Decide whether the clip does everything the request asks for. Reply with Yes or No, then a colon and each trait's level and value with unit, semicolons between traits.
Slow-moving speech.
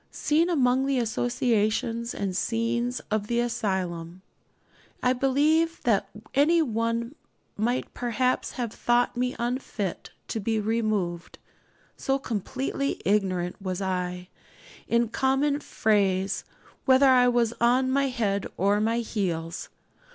Yes: slow, 120 wpm